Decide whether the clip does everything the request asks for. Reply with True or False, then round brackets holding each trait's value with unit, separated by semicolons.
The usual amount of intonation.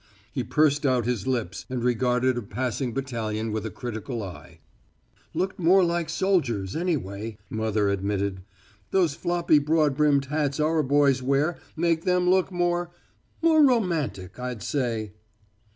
False (7.0 semitones)